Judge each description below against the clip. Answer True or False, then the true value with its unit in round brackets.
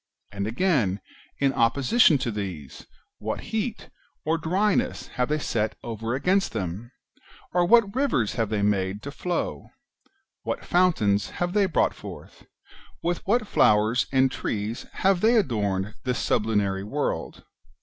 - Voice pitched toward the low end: True (125 Hz)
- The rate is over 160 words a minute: False (140 wpm)